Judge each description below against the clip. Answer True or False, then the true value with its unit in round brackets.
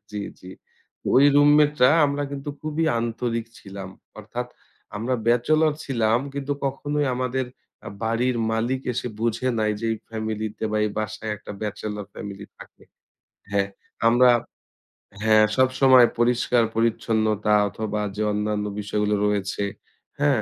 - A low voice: True (115 Hz)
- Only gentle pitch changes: False (3.4 semitones)